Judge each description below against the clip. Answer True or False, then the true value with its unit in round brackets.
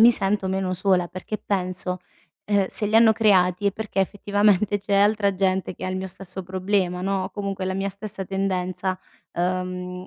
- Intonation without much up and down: True (1.7 semitones)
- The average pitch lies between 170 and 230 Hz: True (190 Hz)